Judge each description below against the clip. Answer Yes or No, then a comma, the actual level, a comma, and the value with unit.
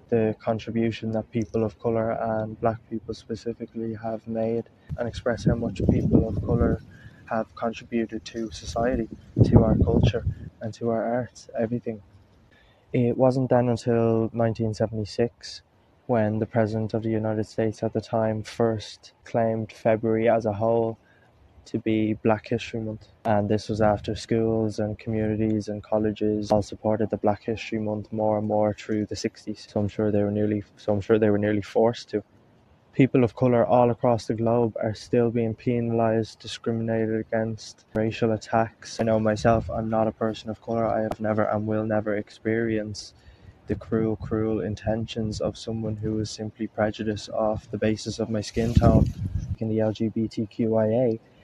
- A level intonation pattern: Yes, narrow, 1.2 semitones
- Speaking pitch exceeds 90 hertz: Yes, low, 110 Hz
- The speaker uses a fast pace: No, average, 165 wpm